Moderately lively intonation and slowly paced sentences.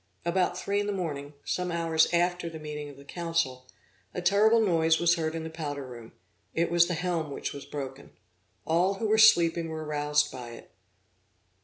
No: average, 3.1 semitones; average, 190 wpm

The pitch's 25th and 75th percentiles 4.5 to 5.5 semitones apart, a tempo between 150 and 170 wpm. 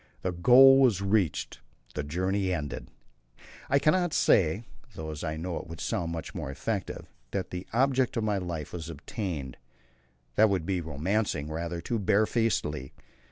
Yes: average, 5.2 semitones; average, 160 wpm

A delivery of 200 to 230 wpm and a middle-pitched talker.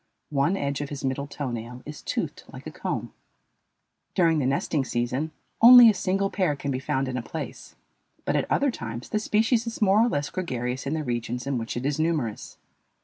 Yes: fast, 205 wpm; medium, 145 Hz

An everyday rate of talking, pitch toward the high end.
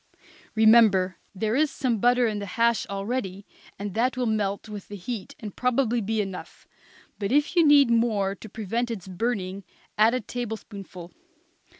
Yes: average, 170 wpm; high, 220 Hz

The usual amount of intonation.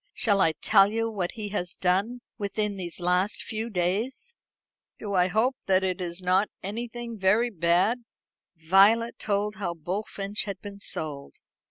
Yes: average, 3.3 semitones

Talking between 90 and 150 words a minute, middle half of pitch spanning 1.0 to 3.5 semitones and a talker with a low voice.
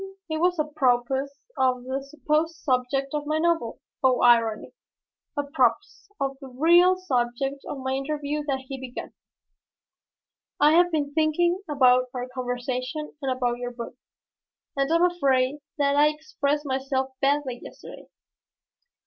No: average, 140 wpm; average, 3.1 semitones; very high, 275 Hz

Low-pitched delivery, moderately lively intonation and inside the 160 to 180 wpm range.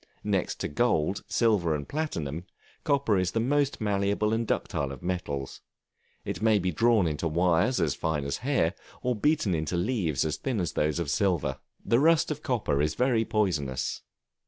No: very low, 95 Hz; wide, 7.1 semitones; average, 175 wpm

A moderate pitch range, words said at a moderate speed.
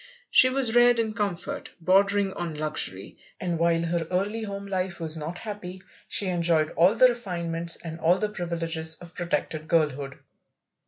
Yes: average, 3.4 semitones; average, 160 wpm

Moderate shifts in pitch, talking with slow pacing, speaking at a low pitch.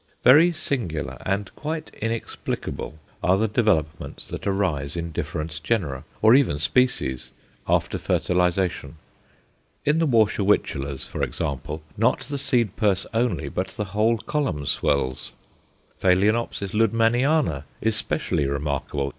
No: wide, 7.1 semitones; slow, 120 wpm; low, 100 Hz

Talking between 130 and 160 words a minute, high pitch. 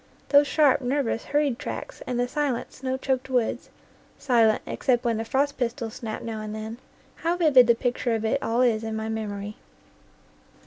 No: average, 180 wpm; high, 245 Hz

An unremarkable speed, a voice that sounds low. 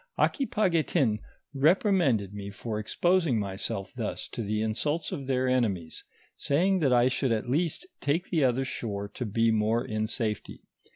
Yes: average, 155 wpm; low, 125 Hz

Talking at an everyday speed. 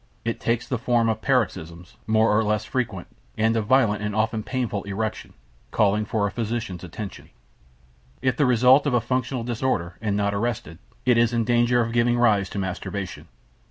Yes: average, 180 wpm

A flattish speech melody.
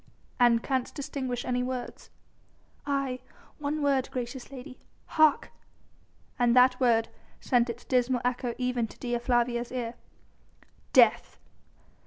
Yes: narrow, 1.5 semitones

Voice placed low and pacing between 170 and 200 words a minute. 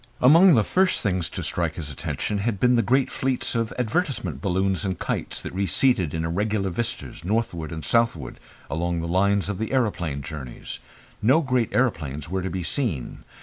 Yes: low, 100 Hz; average, 180 wpm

